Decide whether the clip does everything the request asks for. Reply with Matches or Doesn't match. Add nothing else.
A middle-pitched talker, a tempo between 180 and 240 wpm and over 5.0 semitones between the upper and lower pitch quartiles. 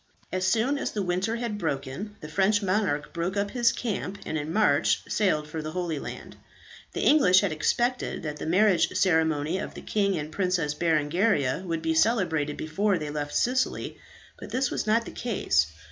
Matches